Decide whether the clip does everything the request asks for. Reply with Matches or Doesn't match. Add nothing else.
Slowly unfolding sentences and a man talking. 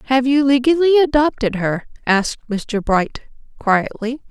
Doesn't match